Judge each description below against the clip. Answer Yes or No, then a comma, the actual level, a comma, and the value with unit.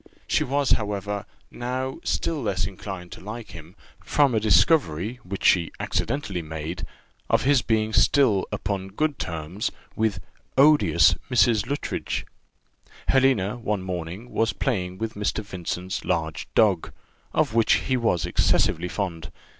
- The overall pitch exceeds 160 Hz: No, low, 105 Hz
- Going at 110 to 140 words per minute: Yes, slow, 135 wpm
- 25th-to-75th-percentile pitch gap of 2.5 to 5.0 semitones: No, wide, 5.4 semitones